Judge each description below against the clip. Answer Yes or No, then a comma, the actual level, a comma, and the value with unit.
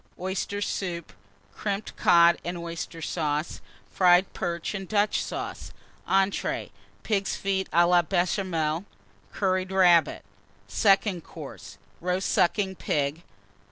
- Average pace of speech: No, slow, 110 wpm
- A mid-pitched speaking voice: Yes, medium, 180 Hz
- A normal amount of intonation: No, narrow, 2.3 semitones